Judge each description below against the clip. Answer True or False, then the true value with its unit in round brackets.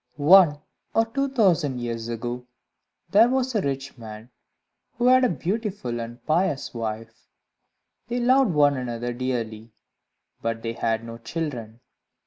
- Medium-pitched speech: False (130 Hz)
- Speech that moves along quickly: False (135 wpm)